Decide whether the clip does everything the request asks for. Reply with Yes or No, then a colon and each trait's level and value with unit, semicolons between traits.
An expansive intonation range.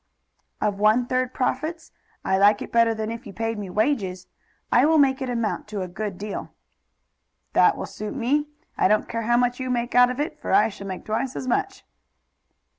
No: average, 3.4 semitones